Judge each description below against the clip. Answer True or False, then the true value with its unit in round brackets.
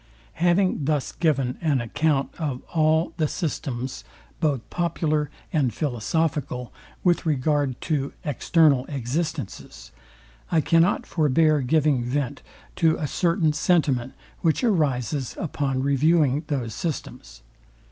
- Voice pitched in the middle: True (150 Hz)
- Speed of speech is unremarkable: False (110 wpm)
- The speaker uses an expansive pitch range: False (3.4 semitones)